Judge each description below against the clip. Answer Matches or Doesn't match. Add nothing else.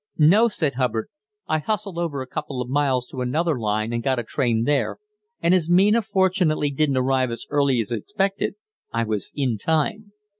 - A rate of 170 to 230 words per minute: Matches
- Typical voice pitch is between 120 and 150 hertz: Matches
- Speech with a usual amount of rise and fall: Doesn't match